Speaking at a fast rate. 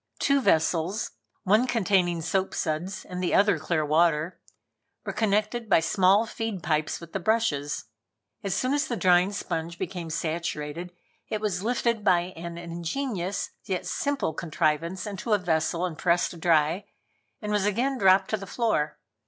No: average, 155 wpm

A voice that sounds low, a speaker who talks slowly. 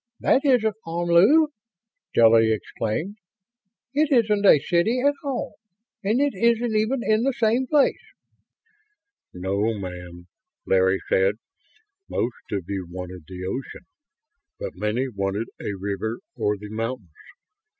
Yes: low, 120 Hz; slow, 125 wpm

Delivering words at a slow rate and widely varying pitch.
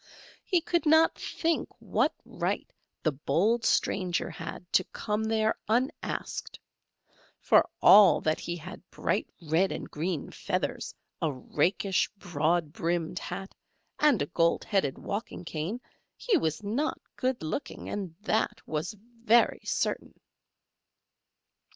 Yes: slow, 120 wpm; wide, 5.7 semitones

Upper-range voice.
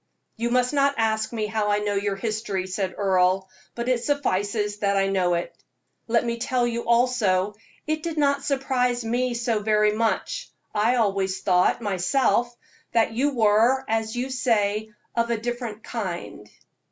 Yes: high, 225 Hz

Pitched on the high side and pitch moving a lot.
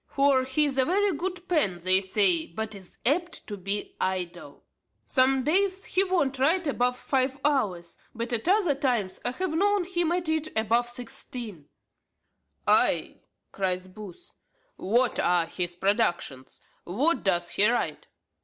Yes: very high, 250 Hz; wide, 8.7 semitones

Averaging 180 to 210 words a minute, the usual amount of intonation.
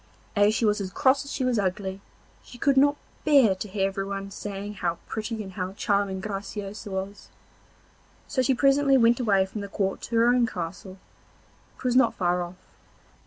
Yes: average, 185 wpm; average, 3.9 semitones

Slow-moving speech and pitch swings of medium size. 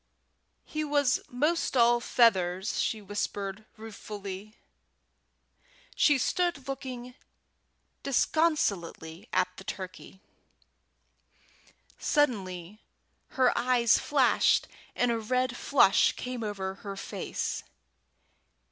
Yes: slow, 85 wpm; average, 4.9 semitones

